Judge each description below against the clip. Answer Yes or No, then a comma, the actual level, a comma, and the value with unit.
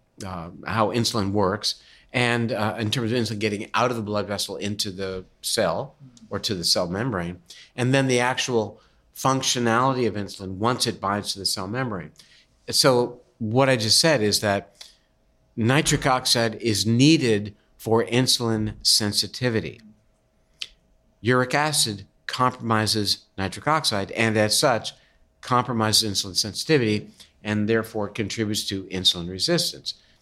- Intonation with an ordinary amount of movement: Yes, average, 3.1 semitones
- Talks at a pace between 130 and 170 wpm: Yes, slow, 135 wpm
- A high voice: No, low, 110 Hz